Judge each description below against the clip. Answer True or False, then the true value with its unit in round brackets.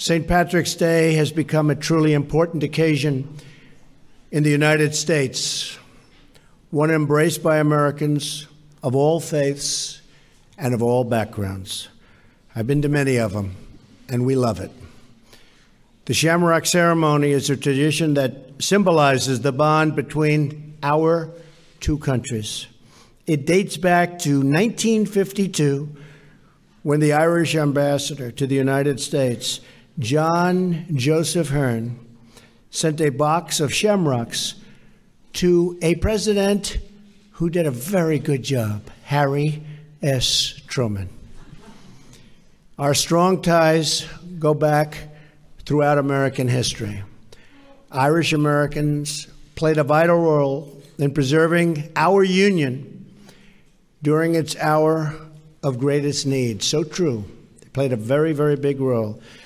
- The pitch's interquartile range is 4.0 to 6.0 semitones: False (2.8 semitones)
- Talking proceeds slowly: True (115 wpm)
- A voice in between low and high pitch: True (150 Hz)